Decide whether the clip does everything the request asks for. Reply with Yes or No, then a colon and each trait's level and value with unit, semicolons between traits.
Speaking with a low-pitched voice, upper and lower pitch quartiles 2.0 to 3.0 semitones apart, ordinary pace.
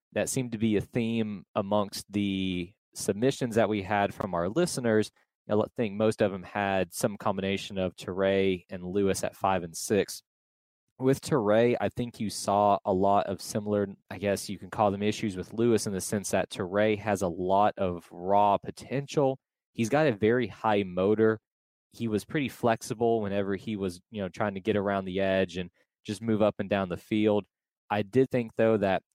Yes: low, 105 Hz; narrow, 2.6 semitones; average, 195 wpm